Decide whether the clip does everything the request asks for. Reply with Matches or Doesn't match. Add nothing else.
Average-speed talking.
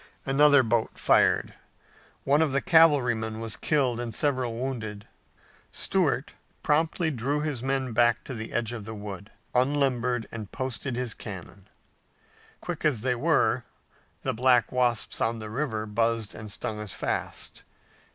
Matches